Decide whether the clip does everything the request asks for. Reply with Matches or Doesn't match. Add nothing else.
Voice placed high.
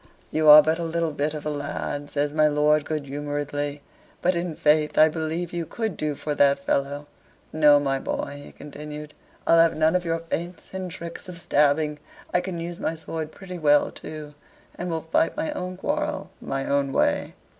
Doesn't match